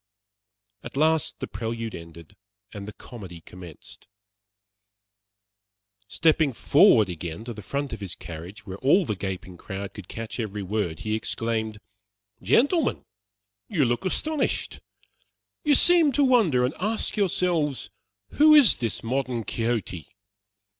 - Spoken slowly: Yes, slow, 130 wpm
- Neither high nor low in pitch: No, low, 115 Hz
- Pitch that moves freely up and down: Yes, wide, 8.3 semitones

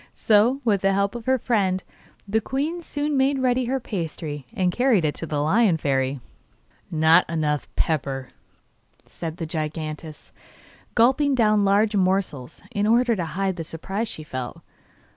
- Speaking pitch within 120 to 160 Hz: No, high, 195 Hz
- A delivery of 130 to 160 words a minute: Yes, average, 155 wpm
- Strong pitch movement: Yes, wide, 6.9 semitones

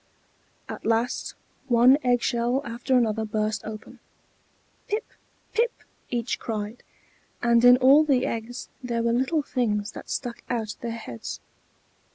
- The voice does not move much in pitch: Yes, narrow, 2.3 semitones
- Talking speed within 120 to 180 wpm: Yes, slow, 135 wpm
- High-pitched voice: Yes, high, 235 Hz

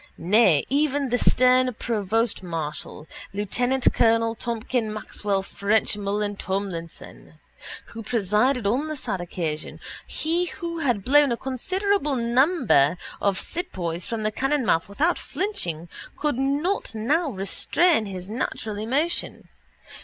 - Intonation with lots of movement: Yes, wide, 5.8 semitones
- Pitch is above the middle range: Yes, high, 230 Hz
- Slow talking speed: Yes, slow, 110 wpm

